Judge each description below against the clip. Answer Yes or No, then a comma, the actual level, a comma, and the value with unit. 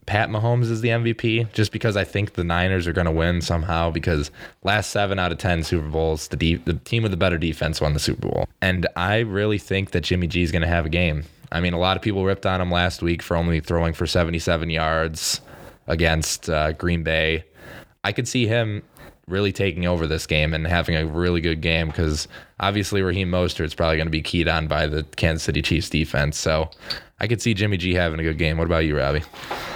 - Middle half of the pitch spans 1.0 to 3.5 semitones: Yes, average, 3.1 semitones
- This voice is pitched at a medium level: No, very low, 85 Hz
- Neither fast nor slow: No, fast, 235 wpm